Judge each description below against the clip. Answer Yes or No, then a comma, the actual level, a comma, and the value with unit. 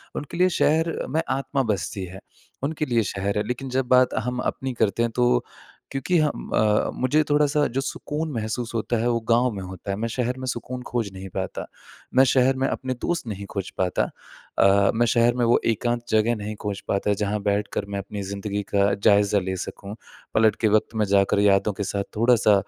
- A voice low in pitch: Yes, low, 115 Hz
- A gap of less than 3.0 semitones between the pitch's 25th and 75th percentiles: No, average, 4.1 semitones